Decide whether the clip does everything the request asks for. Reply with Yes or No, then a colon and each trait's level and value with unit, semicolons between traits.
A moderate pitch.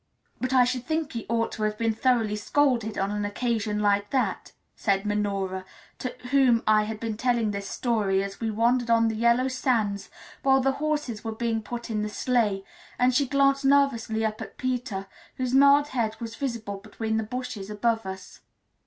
No: high, 230 Hz